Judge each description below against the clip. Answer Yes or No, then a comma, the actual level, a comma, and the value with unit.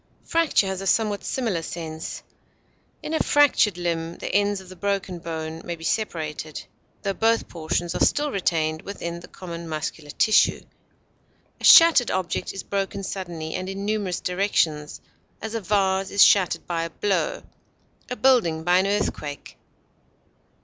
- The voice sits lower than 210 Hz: Yes, medium, 185 Hz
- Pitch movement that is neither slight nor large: Yes, average, 3.7 semitones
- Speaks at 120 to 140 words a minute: No, average, 155 wpm